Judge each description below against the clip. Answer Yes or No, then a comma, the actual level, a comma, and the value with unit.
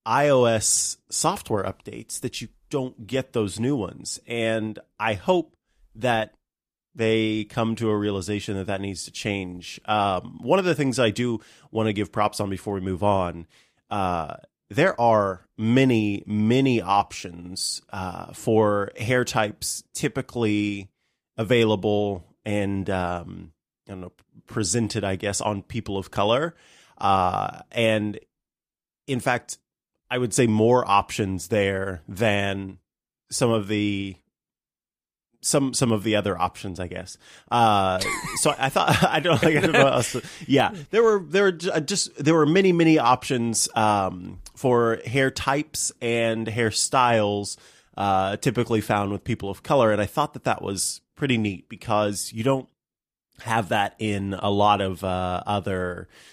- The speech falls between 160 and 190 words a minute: No, average, 150 wpm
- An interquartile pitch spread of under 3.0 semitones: No, average, 3.9 semitones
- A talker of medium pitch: No, low, 110 Hz